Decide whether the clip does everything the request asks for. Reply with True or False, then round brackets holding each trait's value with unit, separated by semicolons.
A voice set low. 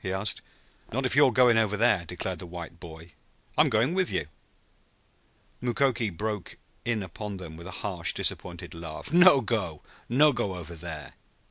True (100 Hz)